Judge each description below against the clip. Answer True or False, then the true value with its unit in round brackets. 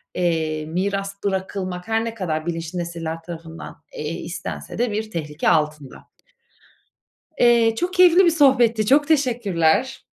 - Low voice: False (190 Hz)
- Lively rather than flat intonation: True (6.2 semitones)